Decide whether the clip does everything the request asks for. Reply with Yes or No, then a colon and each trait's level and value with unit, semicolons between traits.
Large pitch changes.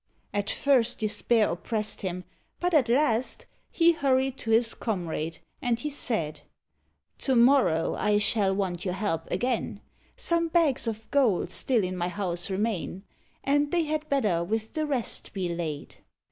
Yes: wide, 6.4 semitones